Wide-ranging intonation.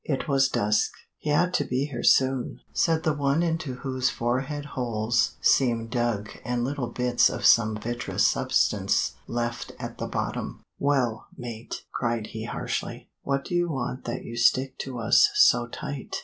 No: average, 3.0 semitones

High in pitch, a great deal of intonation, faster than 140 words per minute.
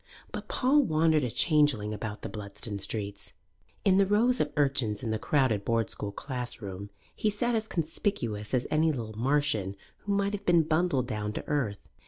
No: low, 135 Hz; wide, 8.3 semitones; average, 180 wpm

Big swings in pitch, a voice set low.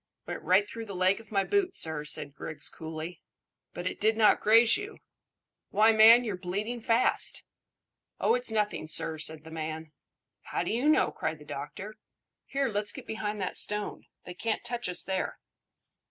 No: wide, 5.8 semitones; high, 205 Hz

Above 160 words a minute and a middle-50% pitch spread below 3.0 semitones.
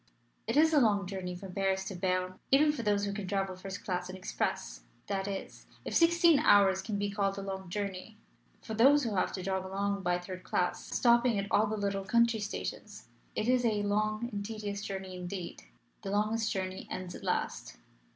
Yes: average, 200 wpm; narrow, 2.4 semitones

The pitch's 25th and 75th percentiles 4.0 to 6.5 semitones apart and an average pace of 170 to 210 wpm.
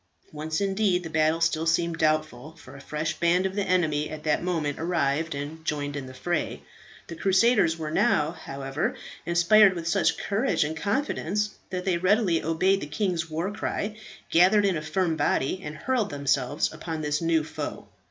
No: average, 3.4 semitones; average, 180 wpm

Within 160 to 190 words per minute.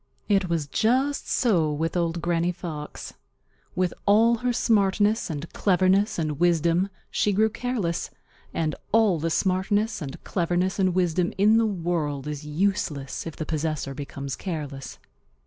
No: average, 145 wpm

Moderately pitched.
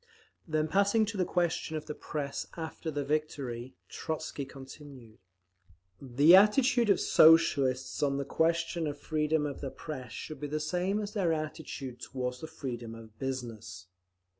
Yes: medium, 150 Hz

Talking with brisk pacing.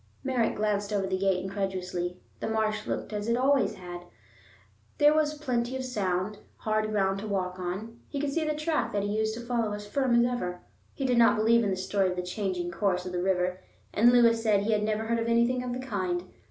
Yes: fast, 235 wpm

